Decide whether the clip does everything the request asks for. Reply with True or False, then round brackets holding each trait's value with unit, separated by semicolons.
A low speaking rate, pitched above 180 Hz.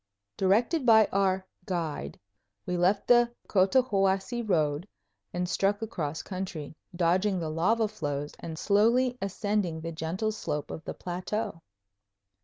True (125 wpm; 190 Hz)